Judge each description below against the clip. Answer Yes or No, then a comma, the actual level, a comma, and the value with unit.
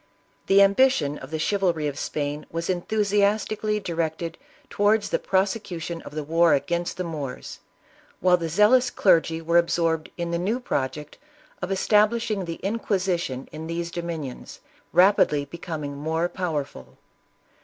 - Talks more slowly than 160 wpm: Yes, average, 145 wpm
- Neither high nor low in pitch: Yes, medium, 170 Hz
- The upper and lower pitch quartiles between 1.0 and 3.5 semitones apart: No, average, 4.0 semitones